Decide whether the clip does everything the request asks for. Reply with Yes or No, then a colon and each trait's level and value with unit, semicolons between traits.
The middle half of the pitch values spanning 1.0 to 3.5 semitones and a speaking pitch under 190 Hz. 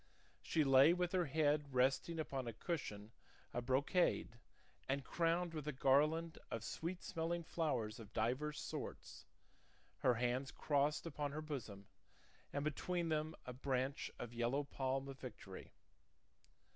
No: average, 4.0 semitones; medium, 140 Hz